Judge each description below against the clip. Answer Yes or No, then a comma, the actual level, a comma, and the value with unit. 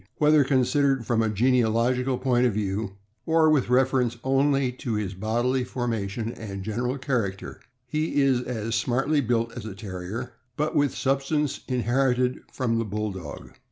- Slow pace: No, average, 150 wpm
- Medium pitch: No, low, 125 Hz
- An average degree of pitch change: Yes, average, 3.3 semitones